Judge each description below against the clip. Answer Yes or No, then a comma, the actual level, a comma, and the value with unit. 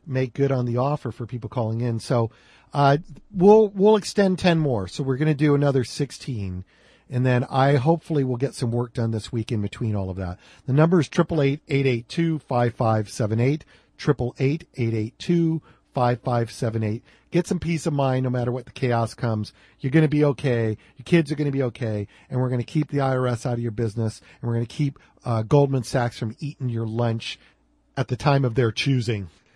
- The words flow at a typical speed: Yes, average, 195 wpm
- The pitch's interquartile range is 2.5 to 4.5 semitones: Yes, average, 3.7 semitones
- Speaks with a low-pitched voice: Yes, low, 125 Hz